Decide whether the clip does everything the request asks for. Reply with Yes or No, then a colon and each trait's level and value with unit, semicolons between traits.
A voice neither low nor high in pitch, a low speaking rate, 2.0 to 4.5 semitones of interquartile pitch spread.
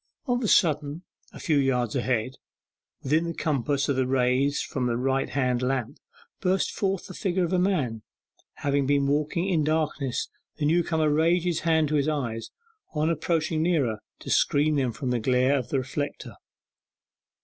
No: medium, 145 Hz; average, 170 wpm; average, 3.8 semitones